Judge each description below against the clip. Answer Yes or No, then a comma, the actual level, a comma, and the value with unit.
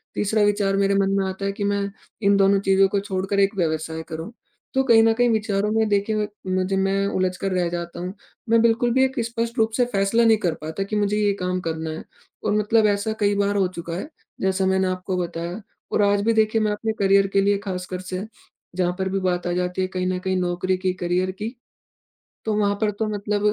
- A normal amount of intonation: No, narrow, 2.3 semitones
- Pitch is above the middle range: Yes, high, 195 Hz